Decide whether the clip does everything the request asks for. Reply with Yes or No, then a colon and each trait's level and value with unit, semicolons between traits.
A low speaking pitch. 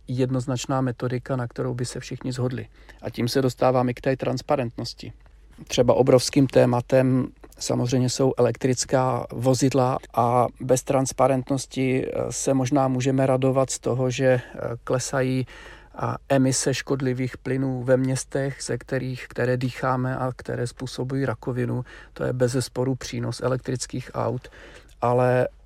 Yes: low, 130 Hz